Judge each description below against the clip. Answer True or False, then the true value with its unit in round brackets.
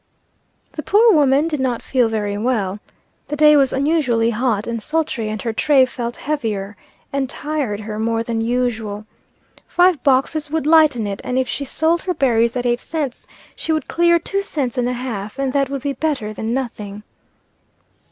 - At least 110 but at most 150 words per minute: False (180 wpm)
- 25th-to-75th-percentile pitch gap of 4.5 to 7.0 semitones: True (4.9 semitones)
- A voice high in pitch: True (255 Hz)